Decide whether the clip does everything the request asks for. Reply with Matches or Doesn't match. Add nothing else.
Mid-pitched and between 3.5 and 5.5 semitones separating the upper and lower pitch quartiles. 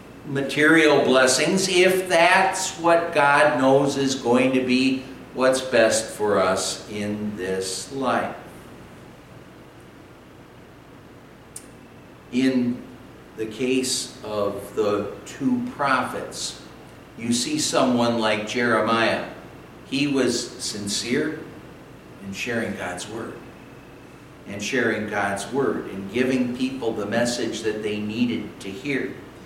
Doesn't match